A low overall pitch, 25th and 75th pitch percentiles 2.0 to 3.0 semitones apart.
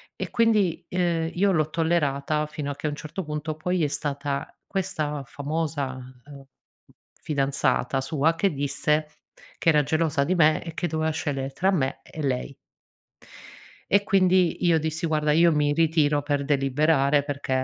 No: medium, 155 Hz; narrow, 2.6 semitones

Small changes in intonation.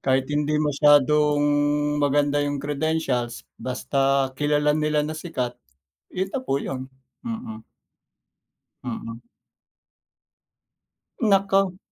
Yes: narrow, 2.3 semitones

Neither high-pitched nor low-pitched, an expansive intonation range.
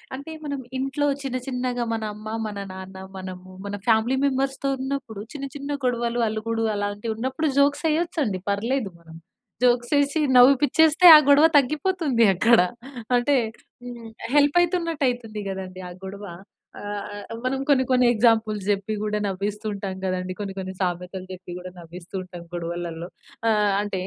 No: high, 225 Hz; wide, 5.8 semitones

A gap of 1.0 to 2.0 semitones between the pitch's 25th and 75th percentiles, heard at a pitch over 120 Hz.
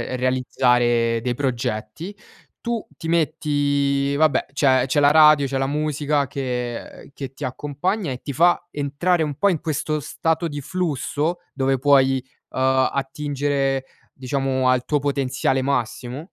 No: average, 2.7 semitones; medium, 140 Hz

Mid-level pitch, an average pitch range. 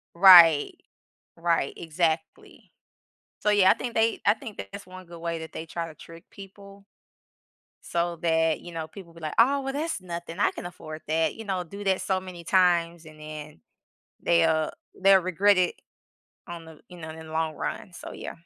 Yes: medium, 170 Hz; average, 3.0 semitones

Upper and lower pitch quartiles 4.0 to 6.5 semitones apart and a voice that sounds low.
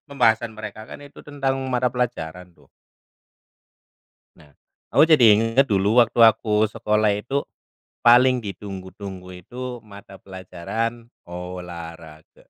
Yes: average, 4.8 semitones; low, 110 Hz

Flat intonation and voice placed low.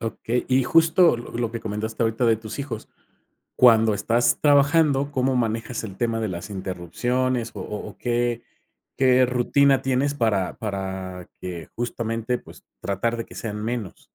No: average, 3.0 semitones; low, 115 Hz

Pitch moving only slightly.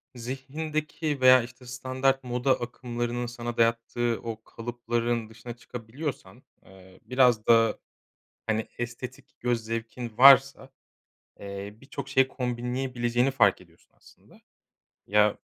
Yes: narrow, 2.1 semitones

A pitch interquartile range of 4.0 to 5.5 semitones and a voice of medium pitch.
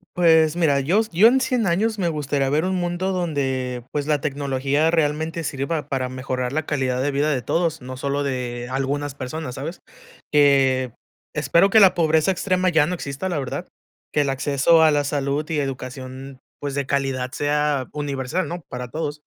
No: average, 3.4 semitones; medium, 145 Hz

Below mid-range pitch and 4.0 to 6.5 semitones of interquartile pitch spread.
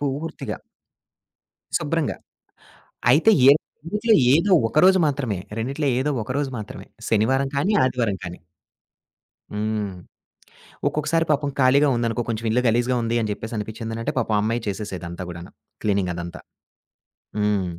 Yes: low, 115 Hz; average, 5.1 semitones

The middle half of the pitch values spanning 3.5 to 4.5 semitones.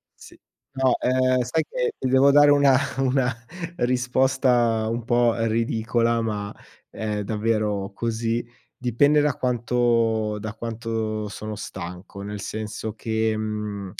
No: average, 2.8 semitones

